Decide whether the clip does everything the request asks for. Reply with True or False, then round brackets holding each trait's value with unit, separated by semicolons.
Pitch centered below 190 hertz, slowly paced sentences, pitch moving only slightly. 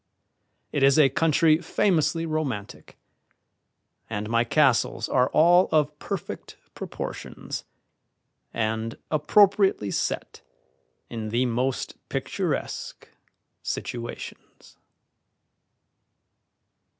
False (140 Hz; 80 wpm; 5.4 semitones)